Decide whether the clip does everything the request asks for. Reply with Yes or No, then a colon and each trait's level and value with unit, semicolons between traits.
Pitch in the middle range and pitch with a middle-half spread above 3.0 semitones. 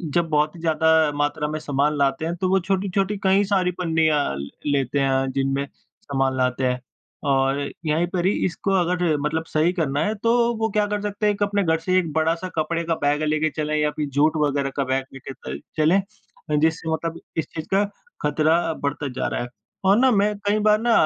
Yes: medium, 160 Hz; average, 4.7 semitones